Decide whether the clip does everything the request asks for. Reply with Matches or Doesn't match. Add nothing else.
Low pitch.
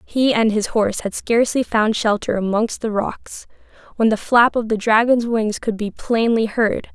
Doesn't match